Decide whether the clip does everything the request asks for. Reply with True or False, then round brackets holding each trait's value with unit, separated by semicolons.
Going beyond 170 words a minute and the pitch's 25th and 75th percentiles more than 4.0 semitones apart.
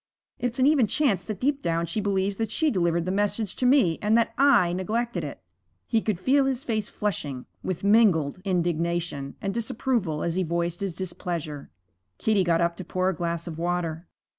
True (190 wpm; 4.7 semitones)